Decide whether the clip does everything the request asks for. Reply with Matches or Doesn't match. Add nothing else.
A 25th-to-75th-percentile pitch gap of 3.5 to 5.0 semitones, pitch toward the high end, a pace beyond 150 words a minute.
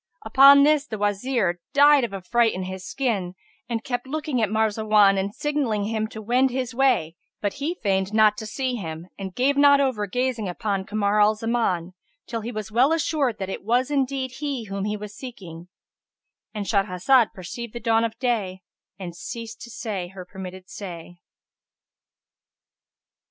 Matches